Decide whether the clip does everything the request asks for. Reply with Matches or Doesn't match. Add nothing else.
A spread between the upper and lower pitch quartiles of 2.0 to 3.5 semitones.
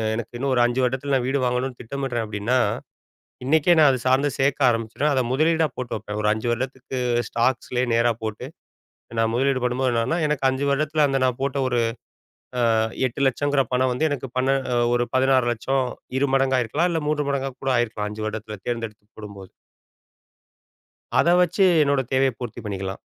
Matches